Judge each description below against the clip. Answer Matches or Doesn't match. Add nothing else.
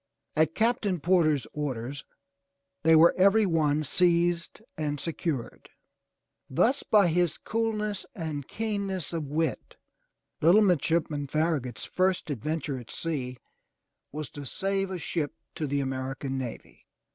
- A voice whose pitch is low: Doesn't match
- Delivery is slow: Matches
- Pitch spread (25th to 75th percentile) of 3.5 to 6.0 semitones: Matches